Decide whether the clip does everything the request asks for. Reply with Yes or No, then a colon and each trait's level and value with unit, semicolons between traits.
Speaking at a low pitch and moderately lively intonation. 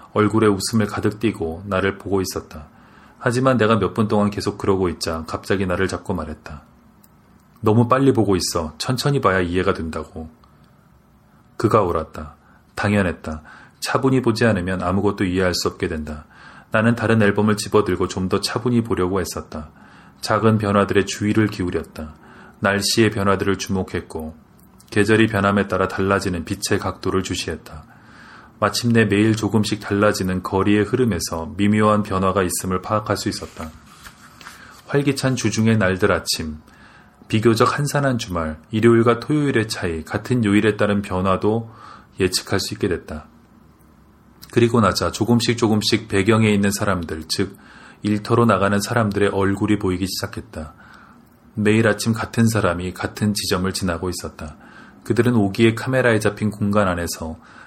Yes: low, 100 Hz; average, 3.1 semitones